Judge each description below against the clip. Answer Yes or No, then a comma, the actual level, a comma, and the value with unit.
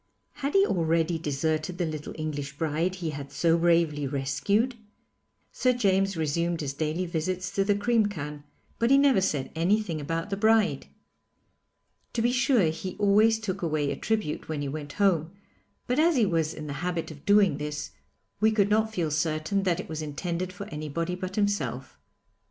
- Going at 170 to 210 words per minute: Yes, average, 180 wpm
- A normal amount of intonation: Yes, average, 4.8 semitones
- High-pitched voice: No, medium, 170 Hz